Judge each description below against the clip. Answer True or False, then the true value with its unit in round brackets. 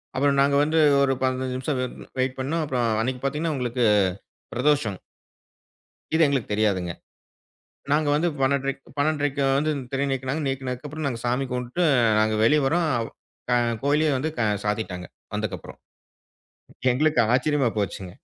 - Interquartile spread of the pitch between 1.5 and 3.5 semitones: True (3.0 semitones)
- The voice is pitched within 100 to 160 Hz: True (135 Hz)